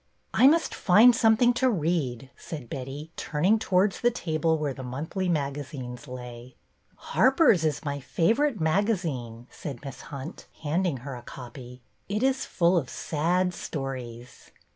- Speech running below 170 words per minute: Yes, average, 150 wpm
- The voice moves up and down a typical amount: No, wide, 6.4 semitones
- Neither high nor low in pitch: Yes, medium, 155 Hz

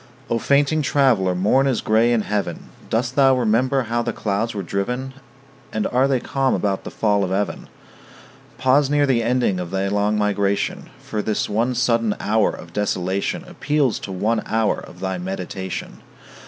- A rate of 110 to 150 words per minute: No, average, 170 wpm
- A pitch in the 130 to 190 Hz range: No, low, 110 Hz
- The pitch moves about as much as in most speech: Yes, average, 4.4 semitones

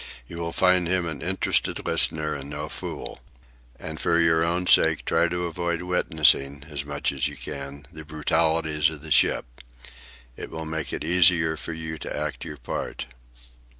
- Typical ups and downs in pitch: No, narrow, 2.0 semitones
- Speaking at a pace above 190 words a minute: No, average, 175 wpm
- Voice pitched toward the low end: Yes, very low, 80 Hz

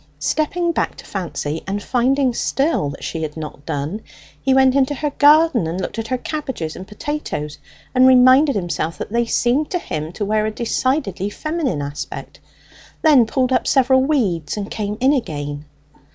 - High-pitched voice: Yes, high, 235 Hz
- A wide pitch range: Yes, wide, 8.3 semitones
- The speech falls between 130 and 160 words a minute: No, average, 175 wpm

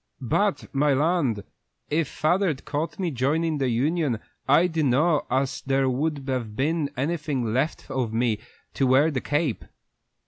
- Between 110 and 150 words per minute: Yes, average, 145 wpm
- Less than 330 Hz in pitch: Yes, medium, 140 Hz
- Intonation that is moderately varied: Yes, average, 3.6 semitones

